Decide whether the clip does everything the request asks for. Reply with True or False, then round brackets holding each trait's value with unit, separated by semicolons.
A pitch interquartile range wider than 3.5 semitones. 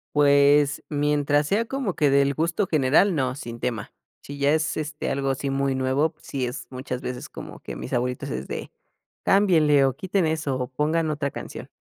False (2.9 semitones)